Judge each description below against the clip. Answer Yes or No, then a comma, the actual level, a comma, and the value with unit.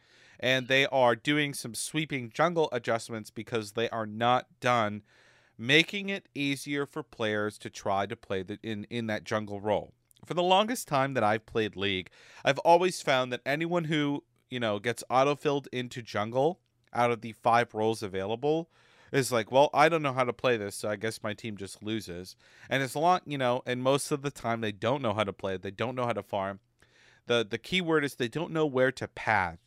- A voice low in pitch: Yes, low, 120 Hz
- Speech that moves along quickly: Yes, fast, 215 wpm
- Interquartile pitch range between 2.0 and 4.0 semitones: No, average, 4.5 semitones